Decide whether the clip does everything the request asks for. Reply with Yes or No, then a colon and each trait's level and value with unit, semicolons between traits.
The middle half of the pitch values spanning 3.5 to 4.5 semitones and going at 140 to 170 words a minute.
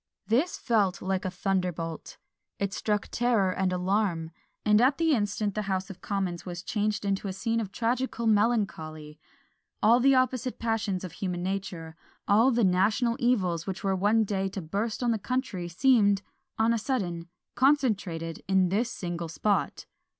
Yes: average, 3.9 semitones; average, 165 wpm